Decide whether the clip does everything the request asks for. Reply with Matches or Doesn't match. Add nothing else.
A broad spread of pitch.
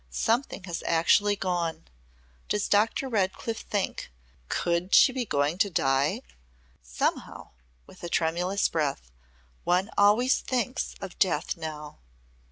Doesn't match